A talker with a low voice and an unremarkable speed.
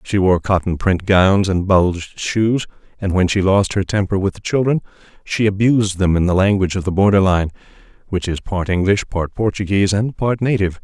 Yes: very low, 95 Hz; average, 190 wpm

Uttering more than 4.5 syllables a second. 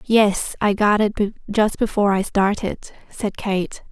No: 4.1 syllables/s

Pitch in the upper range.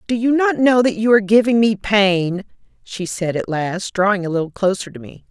Yes: high, 205 Hz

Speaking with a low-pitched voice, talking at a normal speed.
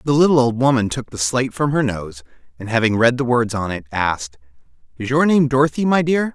No: low, 125 Hz; fast, 225 wpm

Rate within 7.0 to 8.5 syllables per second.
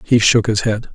No: 4.9 syllables/s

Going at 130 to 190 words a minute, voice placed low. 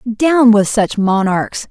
No: average, 140 wpm; high, 220 Hz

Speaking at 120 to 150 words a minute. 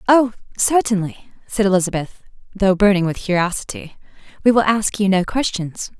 Yes: average, 140 wpm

